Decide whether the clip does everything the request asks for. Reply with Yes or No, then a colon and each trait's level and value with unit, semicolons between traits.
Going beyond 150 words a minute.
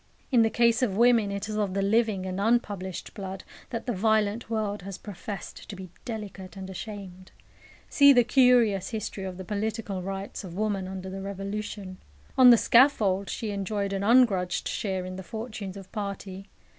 Yes: average, 180 wpm